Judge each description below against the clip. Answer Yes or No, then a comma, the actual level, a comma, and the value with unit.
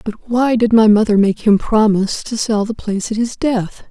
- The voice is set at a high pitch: Yes, high, 220 Hz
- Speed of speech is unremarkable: No, fast, 230 wpm